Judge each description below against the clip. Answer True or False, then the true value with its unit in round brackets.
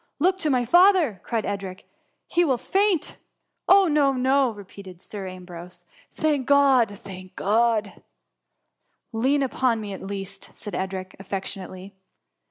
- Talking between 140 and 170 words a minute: True (165 wpm)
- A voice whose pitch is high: True (225 Hz)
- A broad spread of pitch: True (6.6 semitones)